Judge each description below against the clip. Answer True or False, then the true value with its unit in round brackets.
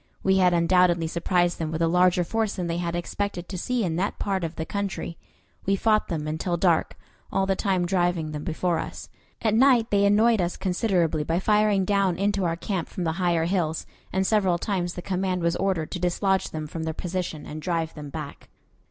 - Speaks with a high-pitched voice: False (180 Hz)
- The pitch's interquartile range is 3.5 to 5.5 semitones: False (2.7 semitones)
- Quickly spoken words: True (210 wpm)